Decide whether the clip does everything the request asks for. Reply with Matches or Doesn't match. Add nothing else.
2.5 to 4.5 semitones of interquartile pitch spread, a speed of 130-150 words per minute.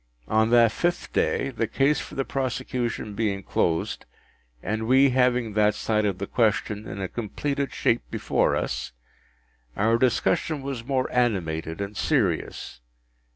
Matches